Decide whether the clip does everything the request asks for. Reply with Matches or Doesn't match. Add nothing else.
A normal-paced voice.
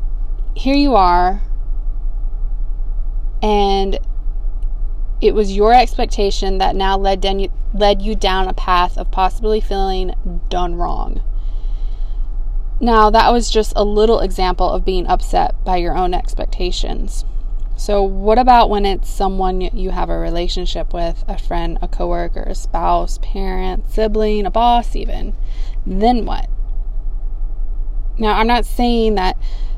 Doesn't match